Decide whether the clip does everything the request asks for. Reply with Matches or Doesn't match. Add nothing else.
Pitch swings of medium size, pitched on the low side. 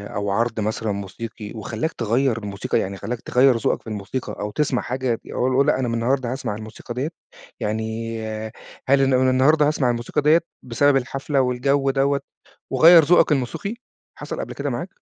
Matches